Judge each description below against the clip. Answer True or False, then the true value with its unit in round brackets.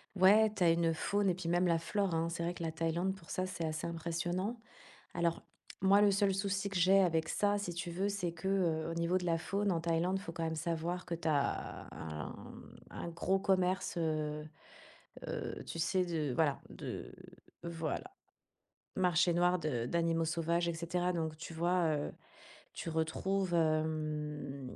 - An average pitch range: False (2.3 semitones)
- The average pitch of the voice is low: False (170 Hz)